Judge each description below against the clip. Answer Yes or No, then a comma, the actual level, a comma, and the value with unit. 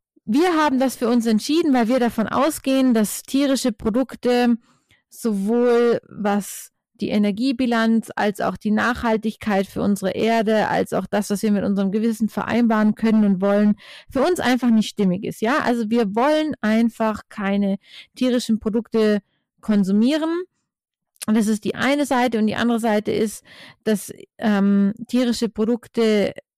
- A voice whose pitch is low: No, high, 225 Hz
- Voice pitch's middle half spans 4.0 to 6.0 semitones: No, average, 2.7 semitones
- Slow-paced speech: No, average, 150 wpm